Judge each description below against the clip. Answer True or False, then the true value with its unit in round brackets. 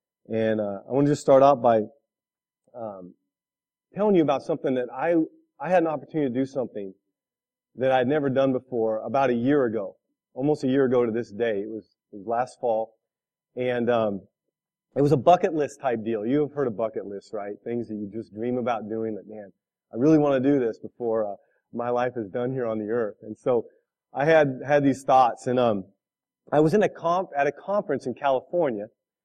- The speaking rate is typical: False (215 wpm)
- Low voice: True (125 Hz)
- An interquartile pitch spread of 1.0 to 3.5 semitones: False (4.7 semitones)